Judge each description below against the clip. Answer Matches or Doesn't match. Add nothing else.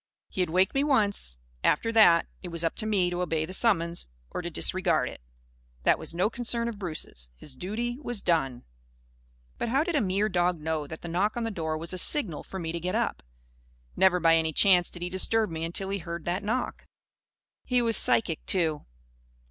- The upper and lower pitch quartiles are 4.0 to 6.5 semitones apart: Matches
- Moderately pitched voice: Matches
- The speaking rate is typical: Doesn't match